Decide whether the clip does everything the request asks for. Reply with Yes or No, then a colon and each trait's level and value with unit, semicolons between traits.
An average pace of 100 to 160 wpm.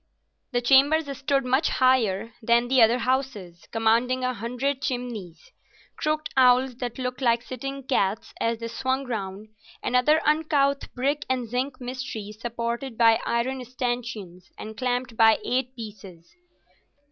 Yes: slow, 135 wpm